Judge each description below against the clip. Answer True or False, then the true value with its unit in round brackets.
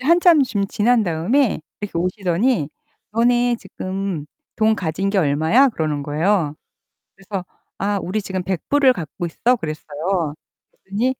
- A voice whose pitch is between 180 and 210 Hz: True (195 Hz)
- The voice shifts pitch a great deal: True (6.2 semitones)